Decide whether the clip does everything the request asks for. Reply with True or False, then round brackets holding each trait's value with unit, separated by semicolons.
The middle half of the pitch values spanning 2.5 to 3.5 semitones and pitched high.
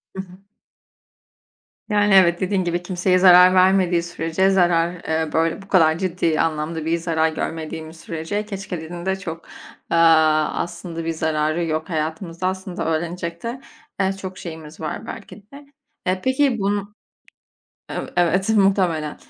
False (2.8 semitones; 175 Hz)